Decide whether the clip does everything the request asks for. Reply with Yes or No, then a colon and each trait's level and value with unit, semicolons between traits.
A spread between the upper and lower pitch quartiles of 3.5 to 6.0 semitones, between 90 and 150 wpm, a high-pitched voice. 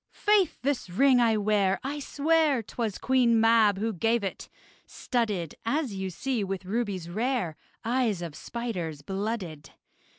Yes: average, 4.5 semitones; average, 140 wpm; high, 225 Hz